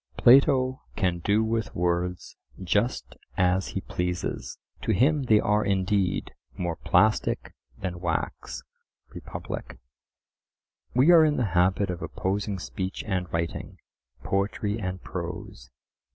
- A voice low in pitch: Yes, very low, 95 Hz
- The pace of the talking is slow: Yes, slow, 120 wpm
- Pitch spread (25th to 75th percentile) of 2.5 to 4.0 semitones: Yes, average, 3.5 semitones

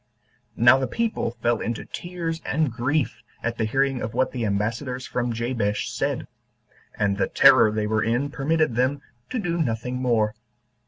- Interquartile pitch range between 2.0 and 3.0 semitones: No, average, 3.9 semitones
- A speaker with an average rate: Yes, average, 165 wpm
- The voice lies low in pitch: Yes, low, 125 Hz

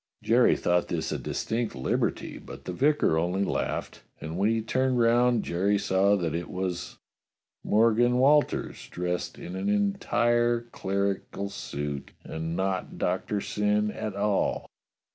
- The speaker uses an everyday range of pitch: Yes, average, 4.9 semitones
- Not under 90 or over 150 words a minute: Yes, average, 140 wpm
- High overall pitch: No, low, 100 Hz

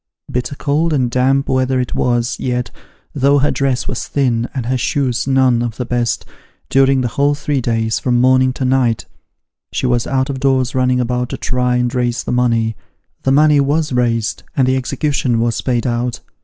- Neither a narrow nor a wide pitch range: No, narrow, 1.8 semitones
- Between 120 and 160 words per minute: No, average, 190 wpm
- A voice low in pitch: Yes, low, 125 Hz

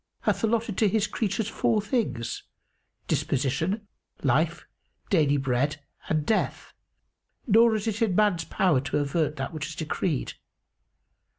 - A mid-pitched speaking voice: Yes, medium, 180 Hz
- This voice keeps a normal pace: No, slow, 130 wpm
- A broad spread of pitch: Yes, wide, 6.8 semitones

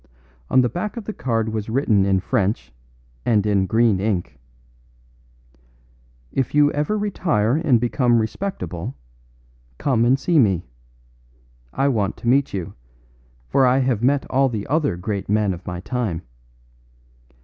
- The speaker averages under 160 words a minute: Yes, average, 145 wpm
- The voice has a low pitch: Yes, low, 115 Hz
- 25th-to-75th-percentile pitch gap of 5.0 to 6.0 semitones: Yes, wide, 5.5 semitones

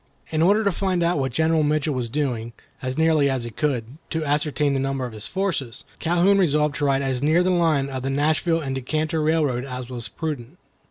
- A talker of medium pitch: Yes, medium, 145 Hz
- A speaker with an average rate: No, fast, 220 wpm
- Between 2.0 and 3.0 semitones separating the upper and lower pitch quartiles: No, average, 3.4 semitones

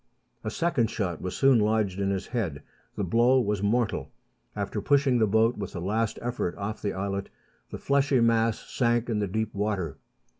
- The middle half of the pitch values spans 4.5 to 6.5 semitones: No, average, 3.1 semitones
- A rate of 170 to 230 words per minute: Yes, average, 185 wpm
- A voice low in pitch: Yes, low, 110 Hz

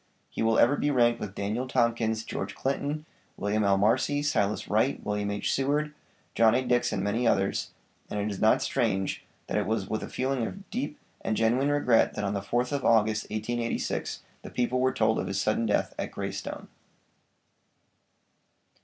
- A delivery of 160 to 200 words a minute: Yes, average, 180 wpm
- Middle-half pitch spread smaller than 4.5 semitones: Yes, average, 3.8 semitones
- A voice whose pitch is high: No, low, 115 Hz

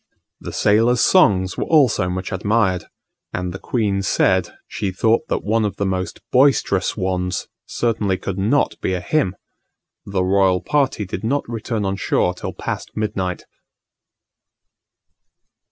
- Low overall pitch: Yes, low, 100 Hz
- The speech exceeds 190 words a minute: No, average, 140 wpm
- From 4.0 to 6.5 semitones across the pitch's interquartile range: No, average, 3.6 semitones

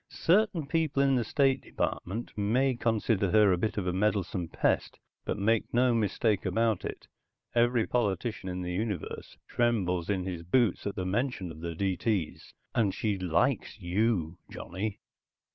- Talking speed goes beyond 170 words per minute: No, average, 160 wpm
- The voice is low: Yes, low, 105 Hz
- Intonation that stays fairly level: No, average, 4.5 semitones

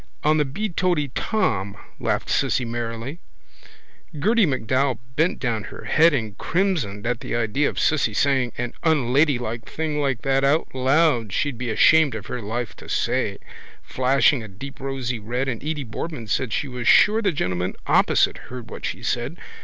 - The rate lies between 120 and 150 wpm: No, average, 165 wpm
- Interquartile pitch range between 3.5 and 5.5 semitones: Yes, average, 4.6 semitones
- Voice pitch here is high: No, low, 130 Hz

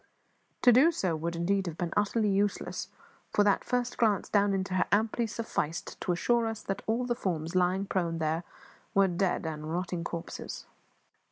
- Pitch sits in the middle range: No, high, 195 Hz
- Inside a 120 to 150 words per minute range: No, average, 175 wpm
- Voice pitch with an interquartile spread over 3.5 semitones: Yes, average, 4.2 semitones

